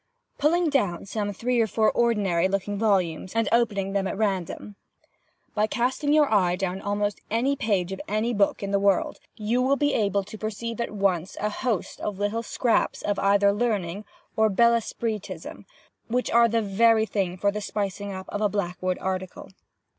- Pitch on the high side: Yes, high, 205 Hz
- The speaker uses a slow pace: No, average, 180 wpm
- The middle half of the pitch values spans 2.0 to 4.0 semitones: Yes, average, 3.0 semitones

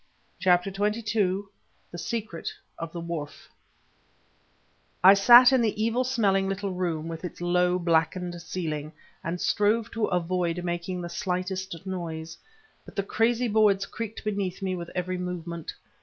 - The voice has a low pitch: No, medium, 185 Hz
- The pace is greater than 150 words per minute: No, average, 140 wpm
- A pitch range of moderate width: Yes, average, 3.1 semitones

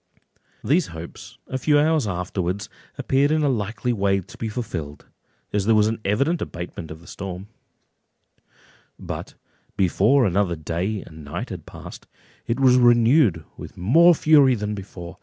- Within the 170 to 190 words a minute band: No, average, 155 wpm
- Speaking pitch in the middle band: No, low, 105 Hz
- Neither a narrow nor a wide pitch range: No, wide, 6.4 semitones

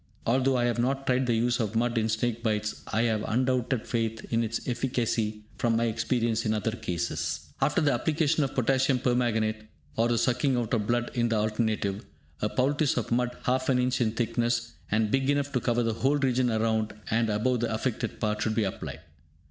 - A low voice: Yes, low, 120 Hz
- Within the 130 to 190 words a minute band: No, fast, 205 wpm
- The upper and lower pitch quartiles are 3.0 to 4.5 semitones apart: No, narrow, 2.4 semitones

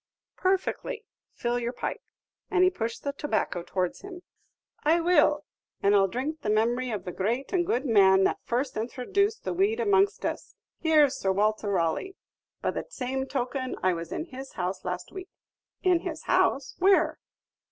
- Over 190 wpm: No, average, 175 wpm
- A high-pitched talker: Yes, very high, 265 Hz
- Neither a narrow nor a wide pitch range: No, wide, 8.9 semitones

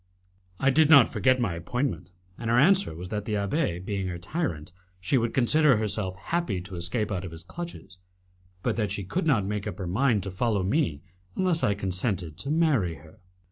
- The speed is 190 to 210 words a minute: Yes, average, 200 wpm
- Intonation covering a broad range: Yes, wide, 6.8 semitones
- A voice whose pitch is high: No, low, 105 Hz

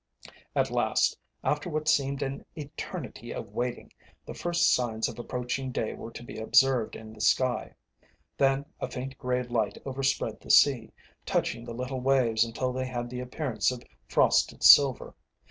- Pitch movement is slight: Yes, narrow, 2.1 semitones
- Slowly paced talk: No, average, 165 wpm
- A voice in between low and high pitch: No, low, 125 Hz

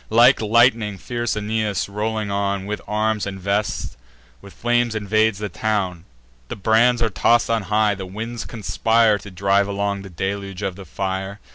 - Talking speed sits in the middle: Yes, average, 160 wpm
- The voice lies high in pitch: No, low, 105 Hz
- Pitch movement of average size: No, narrow, 2.1 semitones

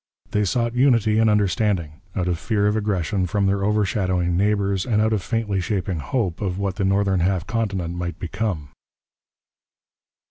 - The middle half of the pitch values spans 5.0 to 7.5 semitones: No, average, 2.9 semitones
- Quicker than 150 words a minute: Yes, average, 165 wpm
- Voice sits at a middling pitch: No, low, 100 Hz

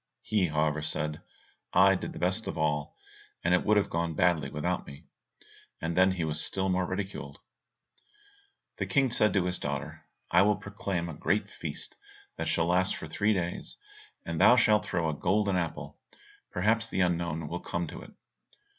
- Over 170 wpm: Yes, average, 180 wpm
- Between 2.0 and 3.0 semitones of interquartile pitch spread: No, average, 3.7 semitones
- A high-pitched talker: No, very low, 90 Hz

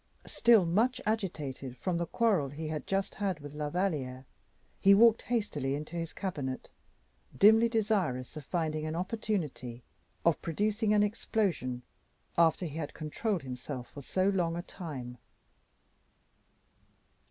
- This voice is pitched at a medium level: Yes, medium, 170 Hz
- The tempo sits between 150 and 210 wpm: No, slow, 135 wpm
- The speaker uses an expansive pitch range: Yes, wide, 6.1 semitones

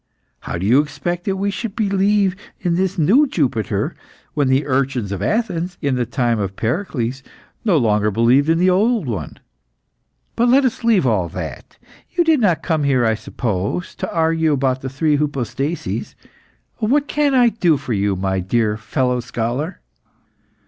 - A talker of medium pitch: Yes, medium, 145 Hz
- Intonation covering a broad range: Yes, wide, 8.4 semitones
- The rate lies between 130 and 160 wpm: No, average, 170 wpm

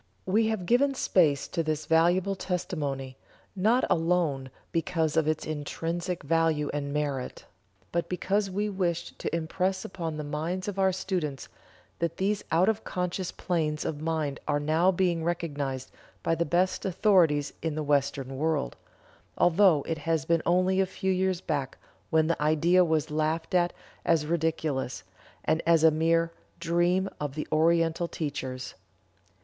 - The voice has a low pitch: No, medium, 165 Hz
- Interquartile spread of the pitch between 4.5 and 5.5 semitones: No, average, 3.2 semitones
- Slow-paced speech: No, average, 155 wpm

